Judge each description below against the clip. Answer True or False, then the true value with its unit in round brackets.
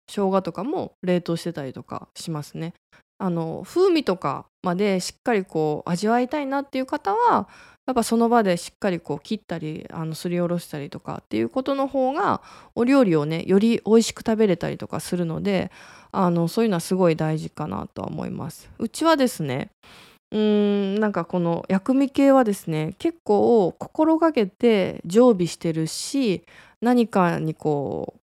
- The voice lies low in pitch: False (195 Hz)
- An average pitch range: False (6.0 semitones)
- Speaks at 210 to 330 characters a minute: False (340 characters per minute)